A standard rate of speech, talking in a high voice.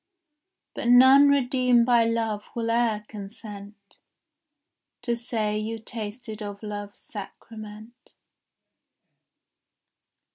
No: slow, 85 wpm; high, 225 Hz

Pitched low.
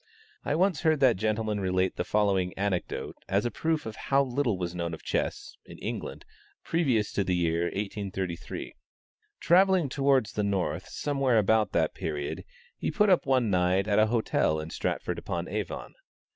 Yes: low, 105 Hz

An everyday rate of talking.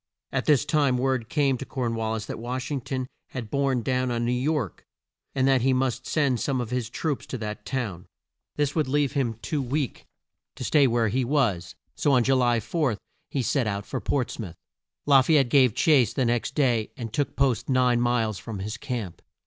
No: fast, 215 wpm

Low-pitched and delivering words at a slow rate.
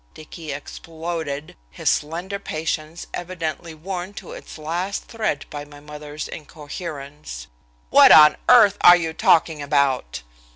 No: medium, 155 Hz; slow, 125 wpm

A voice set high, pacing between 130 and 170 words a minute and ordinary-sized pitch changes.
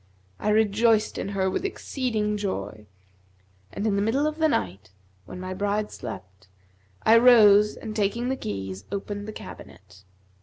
Yes: high, 205 Hz; average, 155 wpm; average, 3.4 semitones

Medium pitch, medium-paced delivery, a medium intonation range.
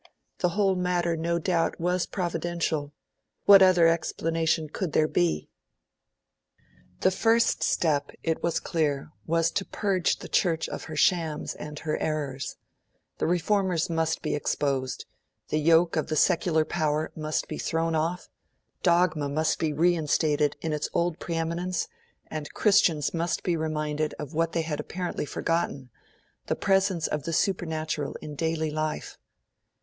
No: medium, 165 Hz; average, 145 wpm; narrow, 2.2 semitones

